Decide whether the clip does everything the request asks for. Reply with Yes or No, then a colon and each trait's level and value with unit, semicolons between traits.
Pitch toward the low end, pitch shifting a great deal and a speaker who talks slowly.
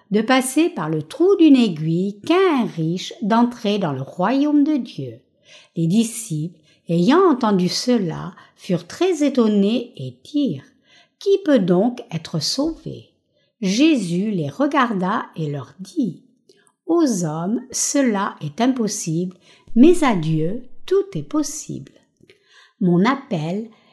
No: high, 215 Hz; wide, 7.6 semitones; slow, 125 wpm